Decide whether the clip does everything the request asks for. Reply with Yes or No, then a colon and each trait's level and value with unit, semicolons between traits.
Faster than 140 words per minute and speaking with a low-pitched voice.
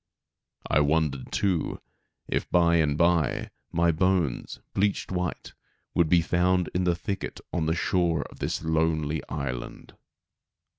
No: slow, 135 wpm; very low, 85 Hz